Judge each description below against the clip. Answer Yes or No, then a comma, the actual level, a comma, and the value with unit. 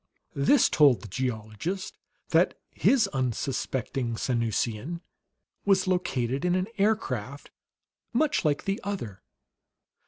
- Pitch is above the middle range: No, medium, 140 Hz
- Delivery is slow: Yes, slow, 100 wpm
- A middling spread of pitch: No, wide, 8.3 semitones